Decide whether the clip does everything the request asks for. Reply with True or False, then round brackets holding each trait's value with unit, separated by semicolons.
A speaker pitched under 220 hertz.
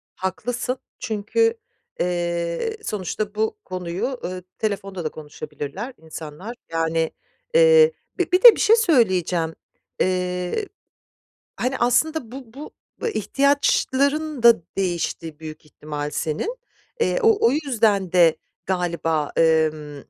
True (190 Hz)